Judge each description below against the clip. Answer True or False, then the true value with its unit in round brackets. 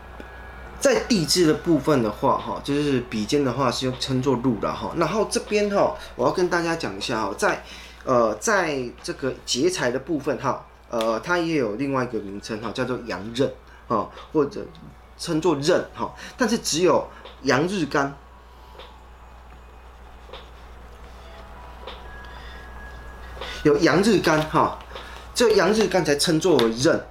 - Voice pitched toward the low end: True (120 Hz)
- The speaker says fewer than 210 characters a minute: True (195 characters per minute)